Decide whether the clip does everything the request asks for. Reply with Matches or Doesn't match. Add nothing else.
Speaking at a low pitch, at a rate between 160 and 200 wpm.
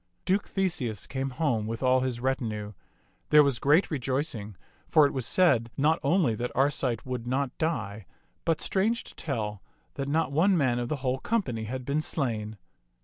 Matches